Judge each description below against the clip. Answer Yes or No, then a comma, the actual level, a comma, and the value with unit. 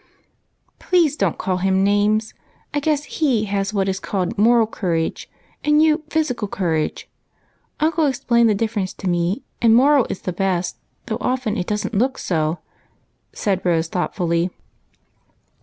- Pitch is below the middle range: No, high, 210 Hz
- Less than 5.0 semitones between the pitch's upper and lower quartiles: No, wide, 5.5 semitones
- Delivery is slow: No, average, 150 wpm